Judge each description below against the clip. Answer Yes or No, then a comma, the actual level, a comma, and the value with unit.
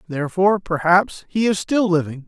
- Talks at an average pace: Yes, average, 160 wpm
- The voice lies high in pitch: No, medium, 180 Hz